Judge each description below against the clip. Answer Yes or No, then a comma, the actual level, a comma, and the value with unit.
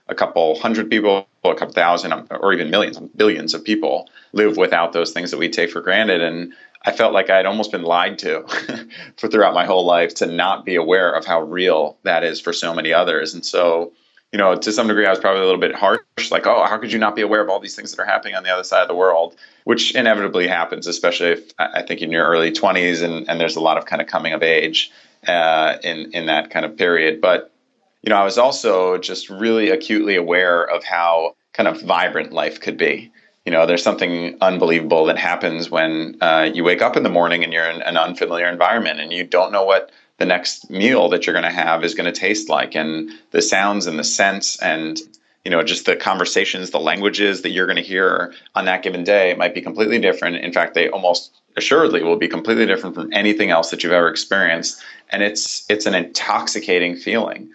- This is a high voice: No, very low, 90 Hz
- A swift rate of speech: Yes, fast, 230 wpm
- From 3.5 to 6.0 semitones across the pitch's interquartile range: Yes, average, 3.8 semitones